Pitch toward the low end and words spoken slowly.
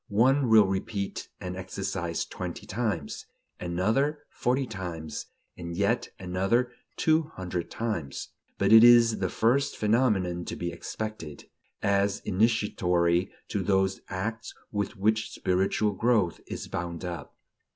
Yes: low, 100 Hz; slow, 125 wpm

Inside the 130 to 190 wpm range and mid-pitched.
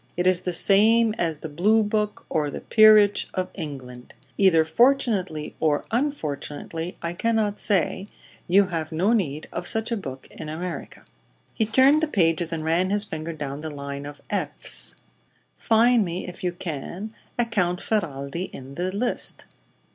Yes: average, 160 wpm; medium, 180 Hz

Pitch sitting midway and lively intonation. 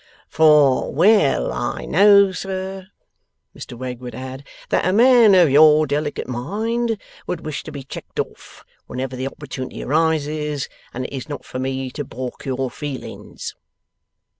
Yes: medium, 145 Hz; wide, 6.0 semitones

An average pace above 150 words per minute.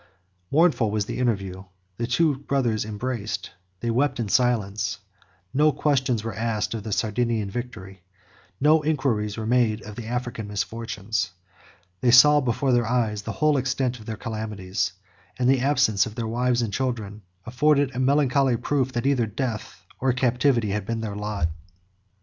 Yes: average, 160 wpm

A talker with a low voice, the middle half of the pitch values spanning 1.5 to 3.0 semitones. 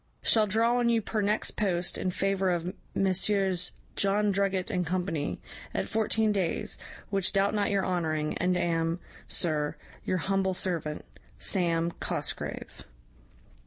No: high, 190 Hz; narrow, 2.6 semitones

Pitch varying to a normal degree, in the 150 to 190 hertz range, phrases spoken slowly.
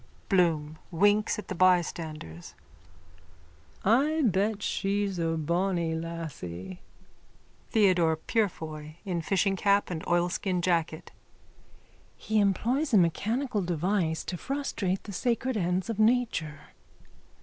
Yes: average, 4.2 semitones; medium, 185 Hz; slow, 105 wpm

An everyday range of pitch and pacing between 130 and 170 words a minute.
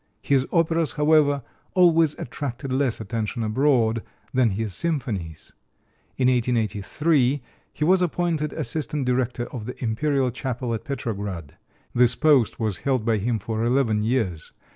Yes: average, 4.6 semitones; slow, 135 wpm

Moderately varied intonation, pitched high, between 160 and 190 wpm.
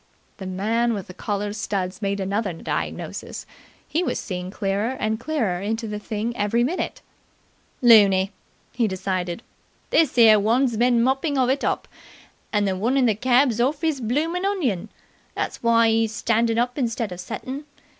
Yes: average, 3.9 semitones; high, 225 Hz; average, 170 wpm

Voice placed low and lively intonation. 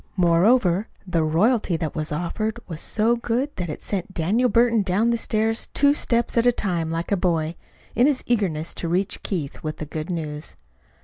No: high, 190 Hz; wide, 5.9 semitones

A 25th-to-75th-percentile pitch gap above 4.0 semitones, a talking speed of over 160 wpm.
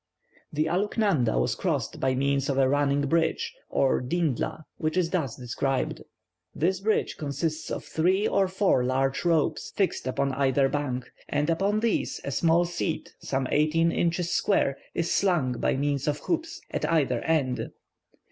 No: average, 4.4 semitones; average, 155 wpm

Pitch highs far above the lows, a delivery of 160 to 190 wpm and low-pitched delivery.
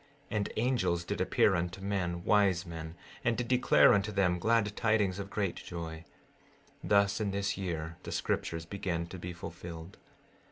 No: average, 3.1 semitones; average, 165 wpm; very low, 95 Hz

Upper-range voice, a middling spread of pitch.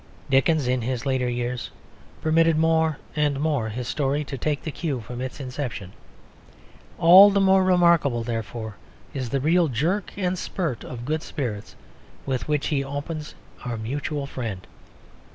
No: medium, 140 Hz; average, 4.5 semitones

